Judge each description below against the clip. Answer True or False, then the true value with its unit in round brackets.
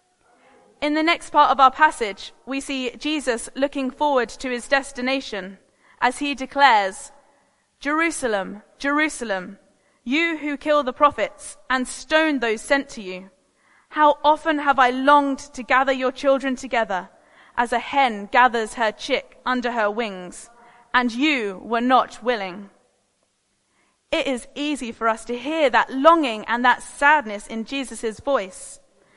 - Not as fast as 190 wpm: True (145 wpm)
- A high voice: True (260 Hz)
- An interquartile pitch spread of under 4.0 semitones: True (3.5 semitones)